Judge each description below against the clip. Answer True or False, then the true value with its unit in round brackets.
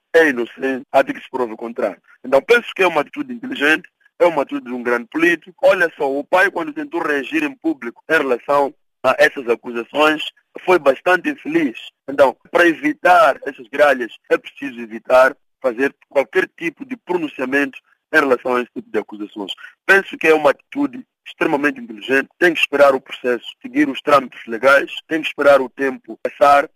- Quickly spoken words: False (185 wpm)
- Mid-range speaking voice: True (145 Hz)